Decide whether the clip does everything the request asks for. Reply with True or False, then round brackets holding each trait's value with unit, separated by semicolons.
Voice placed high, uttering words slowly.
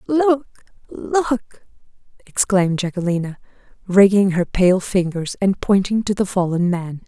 True (195 Hz; 110 wpm)